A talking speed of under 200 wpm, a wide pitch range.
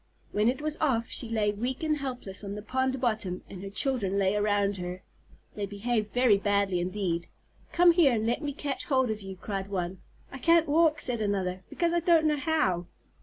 No: fast, 205 wpm; wide, 5.7 semitones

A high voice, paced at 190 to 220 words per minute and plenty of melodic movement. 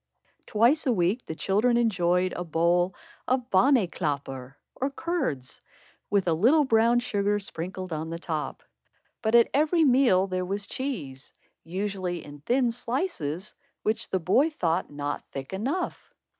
No: high, 195 Hz; average, 145 wpm; wide, 6.5 semitones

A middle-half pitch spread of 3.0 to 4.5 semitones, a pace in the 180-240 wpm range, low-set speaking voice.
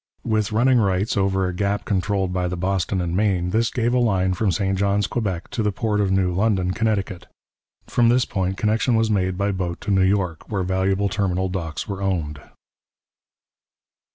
No: narrow, 2.4 semitones; average, 185 wpm; very low, 95 Hz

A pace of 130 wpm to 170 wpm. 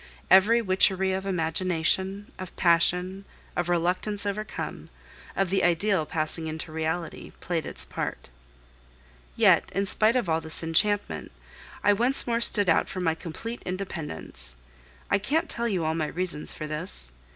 Yes: average, 150 wpm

